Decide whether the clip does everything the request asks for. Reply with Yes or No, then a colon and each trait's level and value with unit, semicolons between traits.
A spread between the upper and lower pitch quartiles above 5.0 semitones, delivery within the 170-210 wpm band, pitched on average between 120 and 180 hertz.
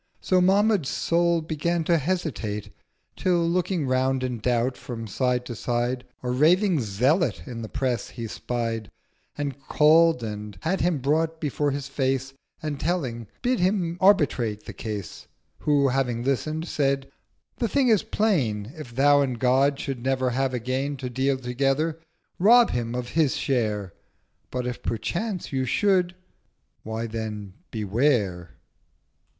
No: wide, 5.4 semitones; average, 145 wpm; low, 135 Hz